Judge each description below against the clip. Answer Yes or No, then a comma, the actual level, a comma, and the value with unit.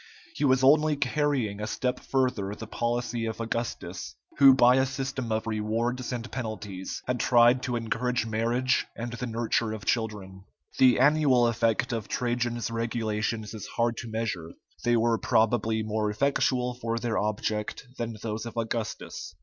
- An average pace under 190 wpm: Yes, average, 155 wpm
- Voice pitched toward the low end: Yes, low, 115 Hz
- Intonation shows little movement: Yes, narrow, 2.2 semitones